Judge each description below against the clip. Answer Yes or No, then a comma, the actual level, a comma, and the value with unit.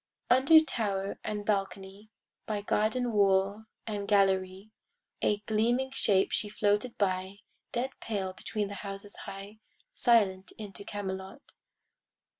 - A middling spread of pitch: No, narrow, 2.0 semitones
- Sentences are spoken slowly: Yes, slow, 115 wpm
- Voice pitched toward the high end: Yes, high, 205 Hz